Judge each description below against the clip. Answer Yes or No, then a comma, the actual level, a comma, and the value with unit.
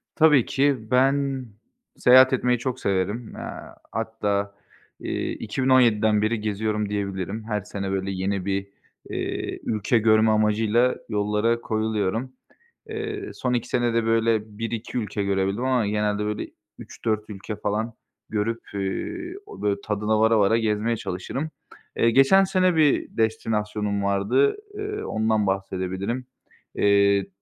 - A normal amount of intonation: Yes, average, 3.2 semitones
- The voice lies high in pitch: No, low, 110 Hz